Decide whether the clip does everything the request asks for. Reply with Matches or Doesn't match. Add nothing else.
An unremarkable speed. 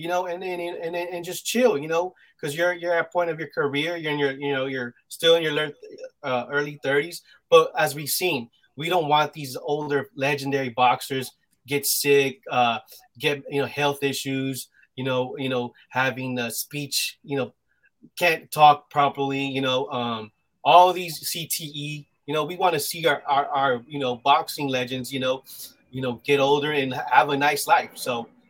Matches